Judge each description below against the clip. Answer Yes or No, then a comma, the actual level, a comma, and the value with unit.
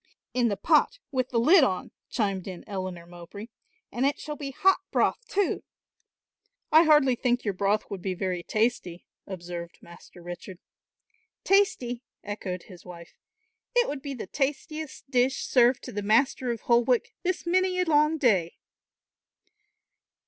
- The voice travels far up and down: Yes, wide, 7.4 semitones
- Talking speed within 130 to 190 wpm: Yes, average, 150 wpm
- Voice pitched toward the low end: No, high, 235 Hz